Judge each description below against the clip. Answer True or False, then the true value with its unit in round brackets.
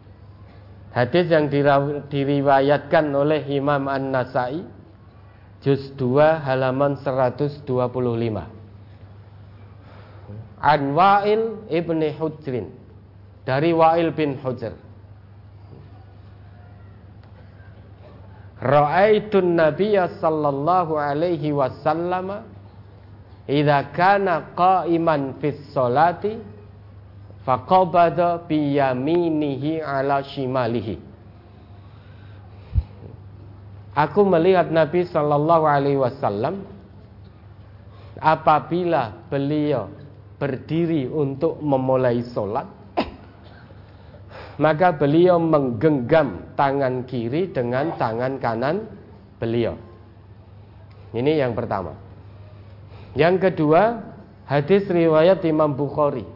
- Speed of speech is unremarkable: False (65 wpm)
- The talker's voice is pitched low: True (130 Hz)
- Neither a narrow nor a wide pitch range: False (7.1 semitones)